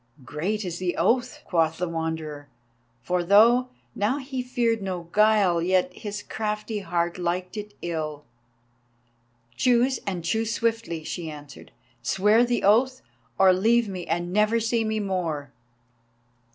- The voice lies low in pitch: No, high, 195 Hz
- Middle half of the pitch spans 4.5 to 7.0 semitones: Yes, average, 4.8 semitones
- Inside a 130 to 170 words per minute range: Yes, average, 140 wpm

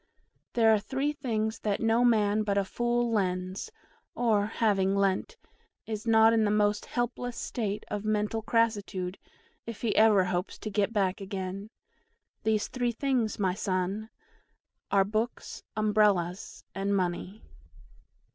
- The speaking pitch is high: Yes, high, 210 Hz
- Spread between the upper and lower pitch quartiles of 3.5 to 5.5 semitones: No, narrow, 2.4 semitones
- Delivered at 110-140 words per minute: Yes, slow, 135 wpm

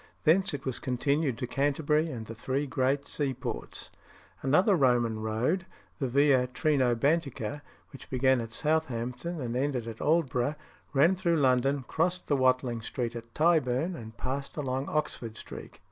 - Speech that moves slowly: No, average, 145 wpm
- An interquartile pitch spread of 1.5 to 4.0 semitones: Yes, average, 3.6 semitones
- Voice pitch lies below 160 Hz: Yes, low, 135 Hz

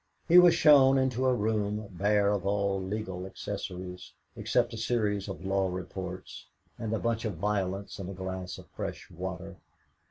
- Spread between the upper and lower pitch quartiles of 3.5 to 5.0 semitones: No, average, 3.0 semitones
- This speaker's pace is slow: No, average, 165 wpm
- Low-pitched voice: Yes, low, 100 Hz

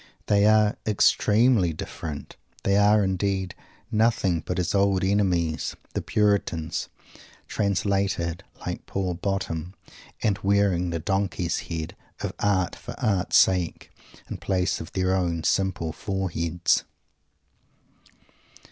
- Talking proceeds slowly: Yes, slow, 110 wpm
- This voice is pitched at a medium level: No, very low, 95 Hz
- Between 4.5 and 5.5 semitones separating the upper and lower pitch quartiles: No, average, 2.8 semitones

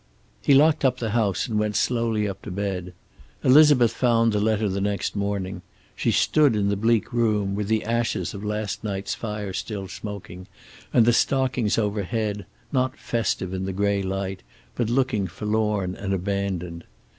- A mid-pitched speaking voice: No, low, 105 Hz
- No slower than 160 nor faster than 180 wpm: Yes, average, 170 wpm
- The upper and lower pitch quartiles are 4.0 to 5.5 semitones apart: No, average, 2.8 semitones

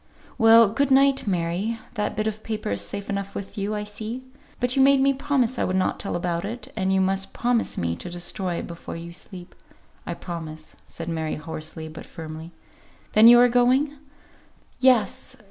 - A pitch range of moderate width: No, wide, 6.0 semitones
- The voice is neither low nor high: No, high, 205 Hz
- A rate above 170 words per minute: Yes, average, 190 wpm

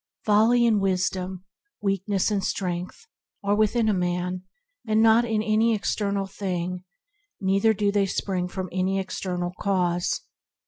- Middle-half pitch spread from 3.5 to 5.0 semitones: No, average, 2.7 semitones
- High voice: Yes, high, 195 Hz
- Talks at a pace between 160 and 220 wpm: No, slow, 135 wpm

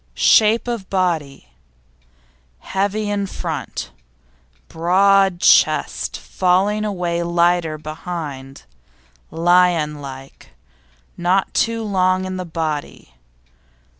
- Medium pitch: Yes, medium, 180 Hz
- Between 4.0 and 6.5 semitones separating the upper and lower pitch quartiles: No, average, 3.4 semitones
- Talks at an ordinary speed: No, slow, 85 wpm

